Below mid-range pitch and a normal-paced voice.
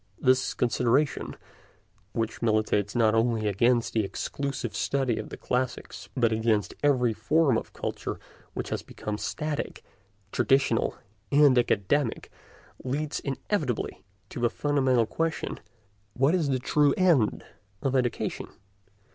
No: low, 125 Hz; slow, 120 wpm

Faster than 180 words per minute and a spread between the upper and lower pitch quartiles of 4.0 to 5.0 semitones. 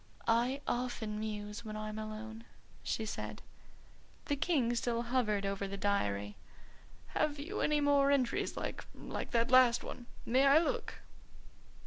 No: average, 140 wpm; average, 4.4 semitones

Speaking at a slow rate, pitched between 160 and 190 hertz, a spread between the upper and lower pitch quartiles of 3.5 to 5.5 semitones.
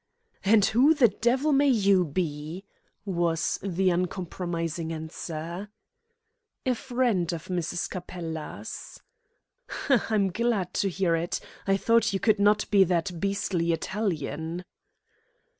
Yes: slow, 120 wpm; medium, 185 Hz; average, 3.8 semitones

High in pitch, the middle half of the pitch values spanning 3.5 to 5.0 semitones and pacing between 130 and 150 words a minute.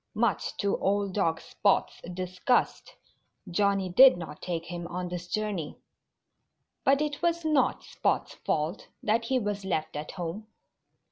Yes: high, 195 Hz; average, 3.9 semitones; average, 140 wpm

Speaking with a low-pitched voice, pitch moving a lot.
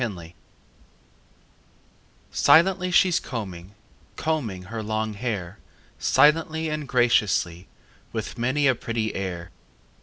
Yes: low, 115 Hz; wide, 7.5 semitones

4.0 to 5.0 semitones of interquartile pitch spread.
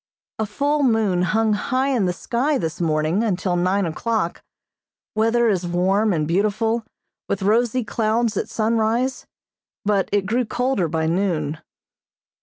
Yes: average, 4.5 semitones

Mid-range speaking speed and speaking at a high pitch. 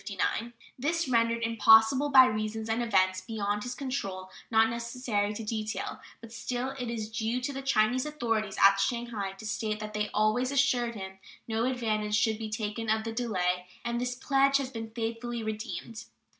Yes: average, 175 wpm; high, 225 Hz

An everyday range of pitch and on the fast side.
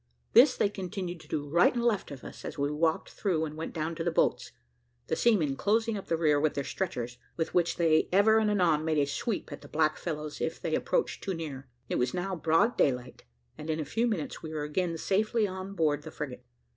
Yes: average, 4.5 semitones; fast, 235 wpm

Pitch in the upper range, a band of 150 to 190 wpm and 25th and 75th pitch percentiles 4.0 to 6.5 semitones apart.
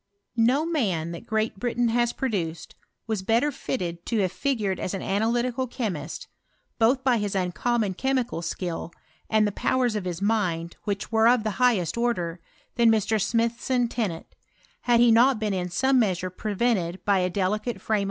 Yes: high, 220 Hz; average, 170 wpm; average, 4.5 semitones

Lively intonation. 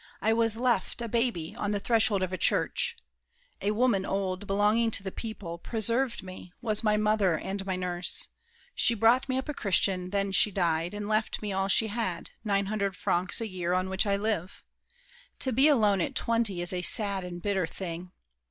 No: average, 3.2 semitones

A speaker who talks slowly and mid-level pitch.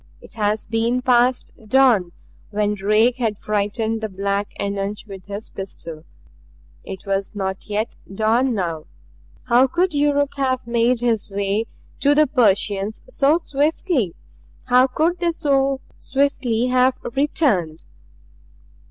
No: slow, 125 wpm; high, 230 Hz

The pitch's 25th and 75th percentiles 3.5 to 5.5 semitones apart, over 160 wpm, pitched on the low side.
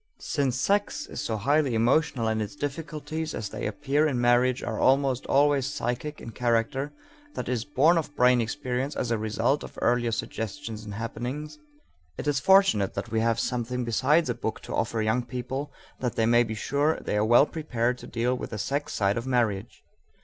Yes: average, 4.1 semitones; average, 195 wpm; low, 125 Hz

